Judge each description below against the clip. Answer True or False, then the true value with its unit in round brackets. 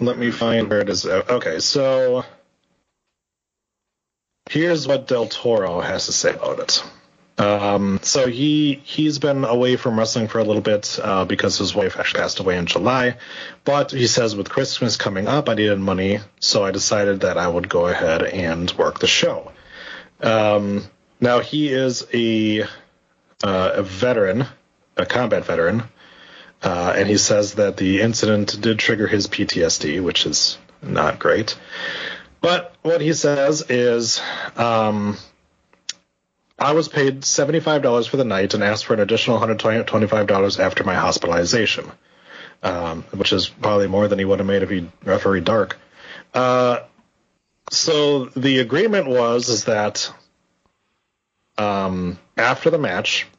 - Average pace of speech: True (150 wpm)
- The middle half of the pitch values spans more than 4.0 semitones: True (4.5 semitones)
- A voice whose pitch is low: True (115 Hz)